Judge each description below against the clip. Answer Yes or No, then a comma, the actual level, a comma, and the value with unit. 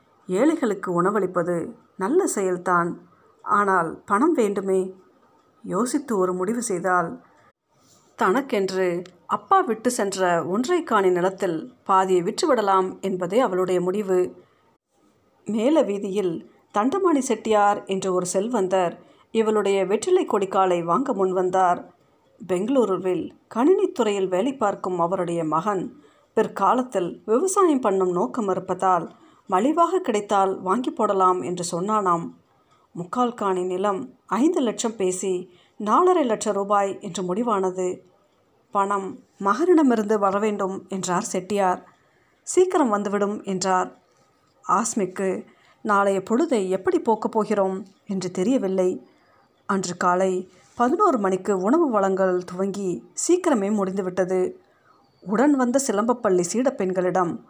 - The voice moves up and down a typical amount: Yes, average, 3.5 semitones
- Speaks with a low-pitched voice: No, high, 195 Hz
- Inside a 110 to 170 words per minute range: No, average, 95 wpm